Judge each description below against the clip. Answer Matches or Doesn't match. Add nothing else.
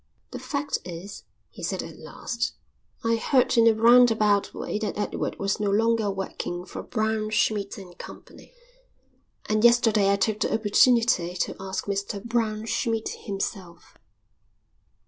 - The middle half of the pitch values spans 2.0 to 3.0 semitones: Matches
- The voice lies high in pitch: Matches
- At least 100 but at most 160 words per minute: Matches